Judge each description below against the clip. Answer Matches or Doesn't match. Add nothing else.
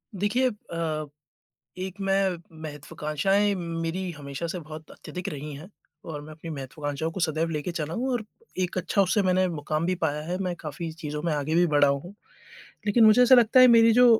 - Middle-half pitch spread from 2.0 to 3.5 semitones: Doesn't match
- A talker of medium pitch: Matches